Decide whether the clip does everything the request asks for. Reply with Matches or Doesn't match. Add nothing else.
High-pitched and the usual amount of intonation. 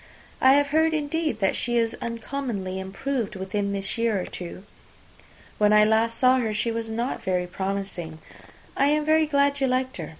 Doesn't match